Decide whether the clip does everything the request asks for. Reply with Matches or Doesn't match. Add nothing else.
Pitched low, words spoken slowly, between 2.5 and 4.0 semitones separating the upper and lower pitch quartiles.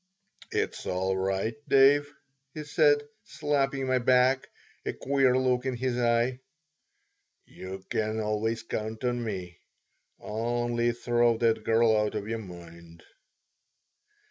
Matches